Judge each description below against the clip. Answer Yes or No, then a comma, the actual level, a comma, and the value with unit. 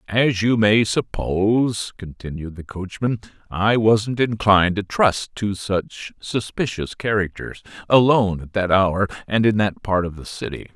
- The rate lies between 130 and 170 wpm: Yes, average, 150 wpm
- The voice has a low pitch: Yes, low, 100 Hz